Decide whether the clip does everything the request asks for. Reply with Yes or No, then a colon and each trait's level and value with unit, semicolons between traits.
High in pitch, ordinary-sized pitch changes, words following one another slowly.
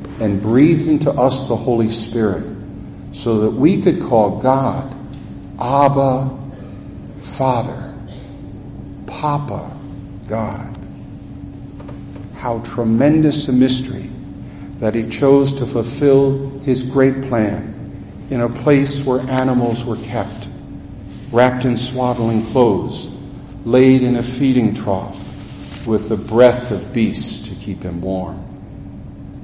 No: low, 125 Hz; average, 3.7 semitones; slow, 110 wpm